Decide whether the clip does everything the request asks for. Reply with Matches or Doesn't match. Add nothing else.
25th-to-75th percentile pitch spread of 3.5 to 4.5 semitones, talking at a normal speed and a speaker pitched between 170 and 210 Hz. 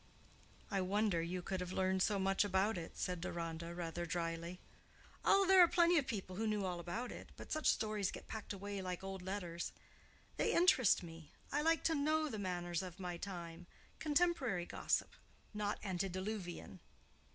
Matches